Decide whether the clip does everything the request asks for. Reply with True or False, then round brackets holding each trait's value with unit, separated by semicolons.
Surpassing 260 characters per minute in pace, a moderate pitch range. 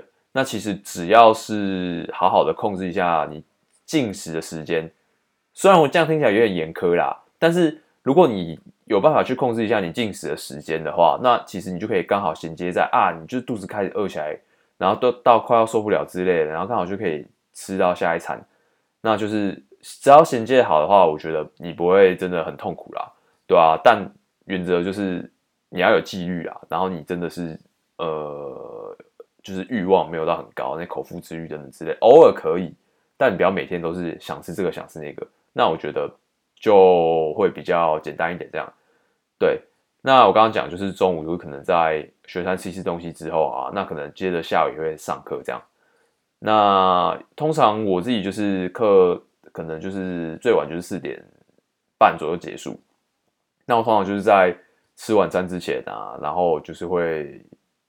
False (280 characters per minute; 6.8 semitones)